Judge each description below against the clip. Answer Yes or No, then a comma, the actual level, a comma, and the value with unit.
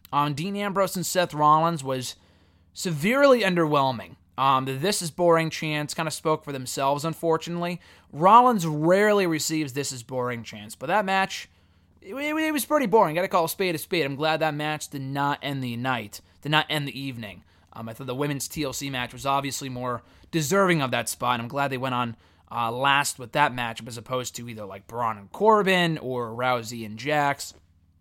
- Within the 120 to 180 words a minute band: No, fast, 205 wpm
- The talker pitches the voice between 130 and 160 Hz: Yes, medium, 140 Hz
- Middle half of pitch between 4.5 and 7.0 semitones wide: Yes, average, 5.2 semitones